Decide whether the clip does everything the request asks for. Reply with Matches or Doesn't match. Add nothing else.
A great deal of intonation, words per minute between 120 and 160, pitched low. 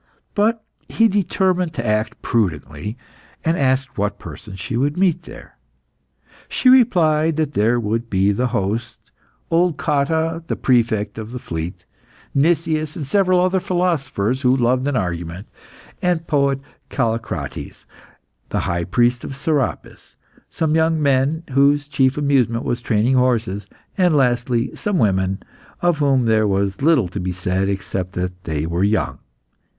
Matches